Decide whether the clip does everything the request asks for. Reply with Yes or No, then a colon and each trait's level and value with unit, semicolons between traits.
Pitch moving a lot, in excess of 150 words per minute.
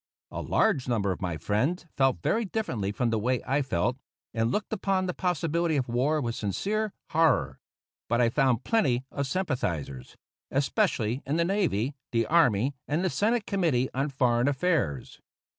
Yes: wide, 6.7 semitones; average, 165 wpm